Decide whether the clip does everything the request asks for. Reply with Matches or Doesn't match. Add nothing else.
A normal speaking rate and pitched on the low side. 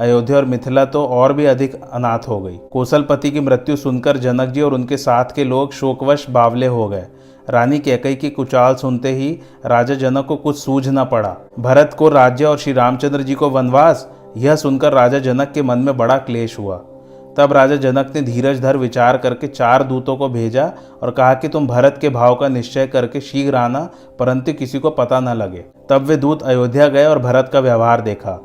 Doesn't match